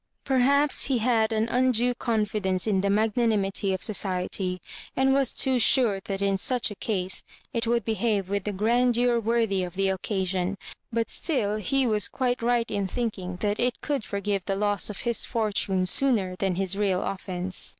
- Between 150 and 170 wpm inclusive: No, average, 180 wpm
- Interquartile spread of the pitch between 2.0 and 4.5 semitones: Yes, average, 3.6 semitones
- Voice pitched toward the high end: Yes, high, 210 Hz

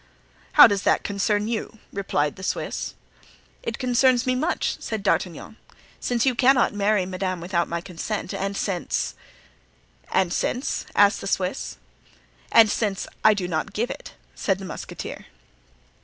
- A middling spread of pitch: Yes, average, 3.7 semitones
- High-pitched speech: Yes, high, 200 Hz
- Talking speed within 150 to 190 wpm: No, average, 140 wpm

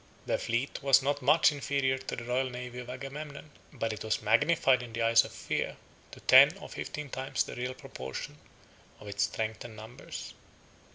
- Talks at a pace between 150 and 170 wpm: No, average, 185 wpm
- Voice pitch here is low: Yes, low, 125 Hz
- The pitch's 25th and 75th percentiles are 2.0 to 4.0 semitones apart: Yes, average, 3.2 semitones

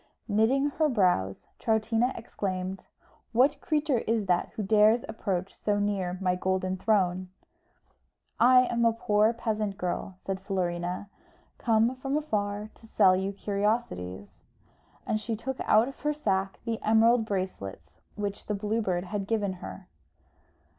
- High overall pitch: Yes, high, 210 Hz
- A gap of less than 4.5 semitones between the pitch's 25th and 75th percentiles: Yes, average, 3.4 semitones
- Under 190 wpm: Yes, average, 145 wpm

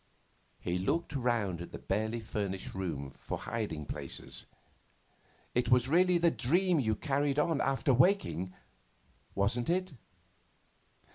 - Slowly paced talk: Yes, slow, 125 wpm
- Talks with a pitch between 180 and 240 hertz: No, low, 120 Hz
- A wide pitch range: Yes, wide, 8.1 semitones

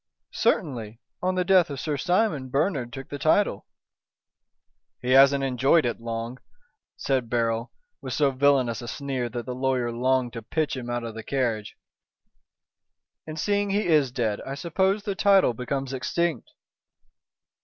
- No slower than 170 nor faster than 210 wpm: No, average, 155 wpm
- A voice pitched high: No, low, 135 Hz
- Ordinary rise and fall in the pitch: Yes, average, 4.7 semitones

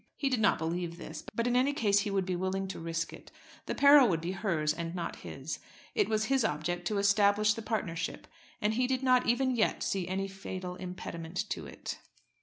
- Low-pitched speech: No, high, 195 Hz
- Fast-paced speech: Yes, fast, 210 wpm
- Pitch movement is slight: No, average, 4.6 semitones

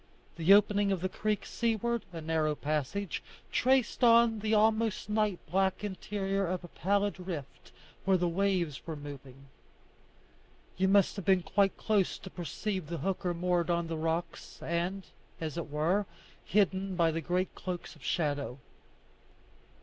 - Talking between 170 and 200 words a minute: No, average, 150 wpm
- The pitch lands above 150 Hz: Yes, medium, 185 Hz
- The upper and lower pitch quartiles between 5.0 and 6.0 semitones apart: No, average, 3.6 semitones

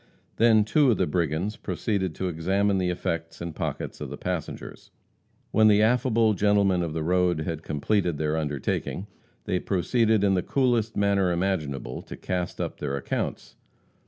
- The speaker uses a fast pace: No, average, 160 wpm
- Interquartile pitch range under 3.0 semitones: No, average, 4.3 semitones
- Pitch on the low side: Yes, very low, 95 Hz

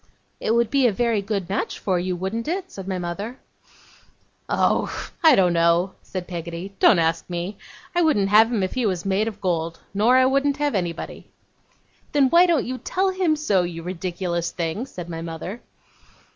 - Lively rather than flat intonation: Yes, wide, 6.4 semitones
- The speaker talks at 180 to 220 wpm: Yes, average, 185 wpm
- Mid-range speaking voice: No, high, 195 Hz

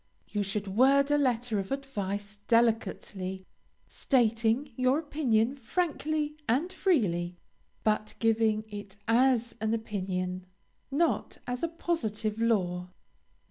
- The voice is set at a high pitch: Yes, high, 225 Hz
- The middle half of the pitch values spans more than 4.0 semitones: Yes, average, 4.8 semitones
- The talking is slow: Yes, slow, 110 wpm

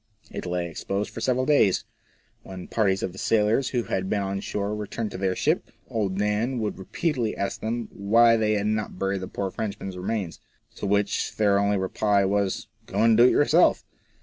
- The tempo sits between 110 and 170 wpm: No, average, 200 wpm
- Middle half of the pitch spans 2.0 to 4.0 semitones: Yes, narrow, 2.5 semitones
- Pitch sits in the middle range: No, low, 105 Hz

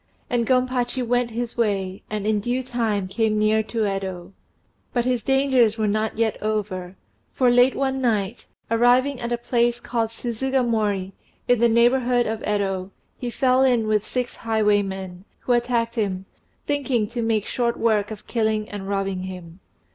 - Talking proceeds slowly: No, average, 160 wpm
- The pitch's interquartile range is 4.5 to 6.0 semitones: No, average, 2.9 semitones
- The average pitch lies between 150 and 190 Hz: No, high, 225 Hz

